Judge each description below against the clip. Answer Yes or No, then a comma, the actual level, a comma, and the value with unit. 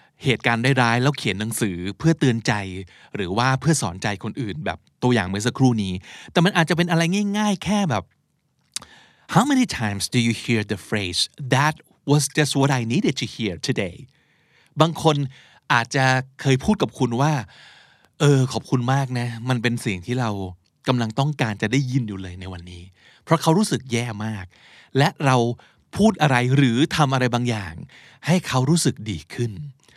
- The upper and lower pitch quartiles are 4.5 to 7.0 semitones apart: Yes, average, 4.8 semitones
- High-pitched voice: No, low, 130 Hz